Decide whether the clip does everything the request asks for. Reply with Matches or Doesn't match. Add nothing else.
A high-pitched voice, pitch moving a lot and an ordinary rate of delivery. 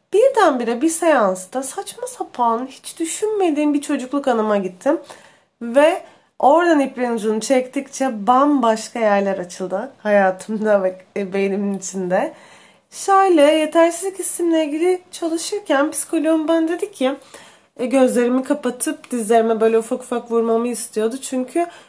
Matches